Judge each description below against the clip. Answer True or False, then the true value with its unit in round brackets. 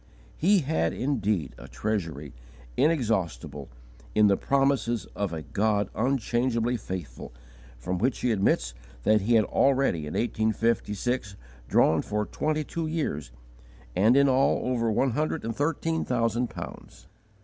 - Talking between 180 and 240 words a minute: False (140 wpm)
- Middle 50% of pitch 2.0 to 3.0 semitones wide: False (5.6 semitones)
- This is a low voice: True (115 Hz)